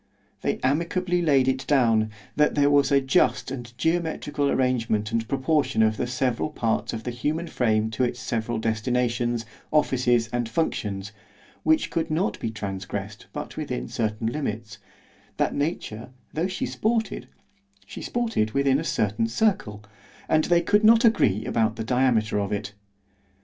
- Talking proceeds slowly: No, average, 145 wpm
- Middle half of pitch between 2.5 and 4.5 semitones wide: No, wide, 5.5 semitones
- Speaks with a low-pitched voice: Yes, low, 125 Hz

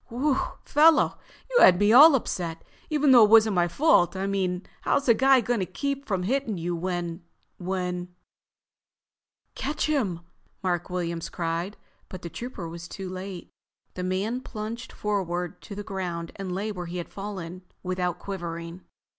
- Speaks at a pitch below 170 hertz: No, high, 190 Hz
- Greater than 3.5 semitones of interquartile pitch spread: Yes, average, 4.5 semitones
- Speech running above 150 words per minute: Yes, average, 160 wpm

